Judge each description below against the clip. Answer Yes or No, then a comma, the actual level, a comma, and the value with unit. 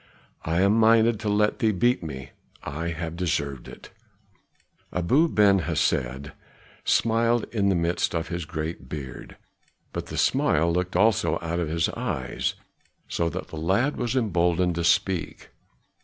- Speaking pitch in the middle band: No, very low, 85 Hz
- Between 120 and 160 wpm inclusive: Yes, average, 150 wpm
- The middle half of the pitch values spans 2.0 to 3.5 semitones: No, average, 4.6 semitones